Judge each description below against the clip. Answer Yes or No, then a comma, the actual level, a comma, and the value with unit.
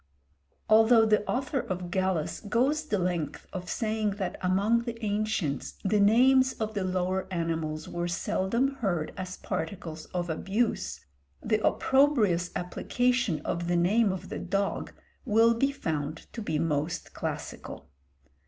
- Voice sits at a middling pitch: No, high, 195 Hz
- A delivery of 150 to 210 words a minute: No, average, 140 wpm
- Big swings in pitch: No, average, 4.7 semitones